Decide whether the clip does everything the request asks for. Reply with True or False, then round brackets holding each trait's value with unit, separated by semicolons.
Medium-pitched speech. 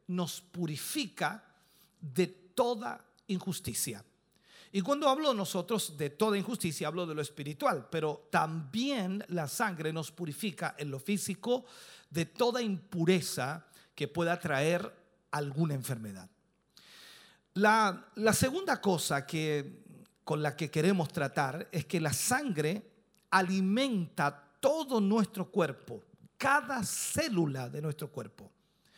True (180 Hz)